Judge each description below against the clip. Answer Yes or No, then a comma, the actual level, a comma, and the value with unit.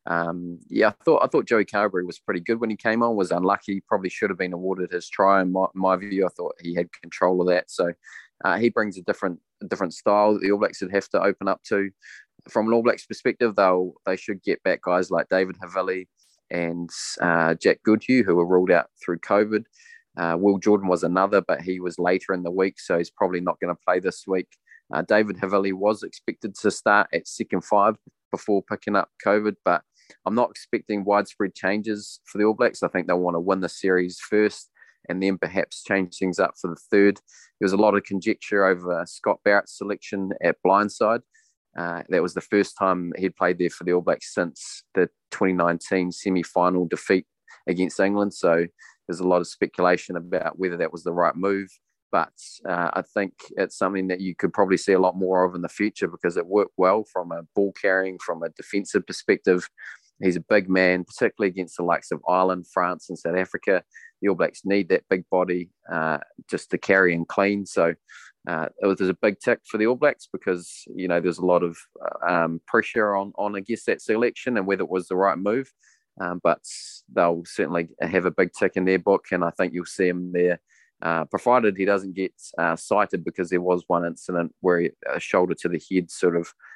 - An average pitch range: No, narrow, 2.0 semitones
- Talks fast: Yes, fast, 220 wpm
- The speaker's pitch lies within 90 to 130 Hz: Yes, very low, 95 Hz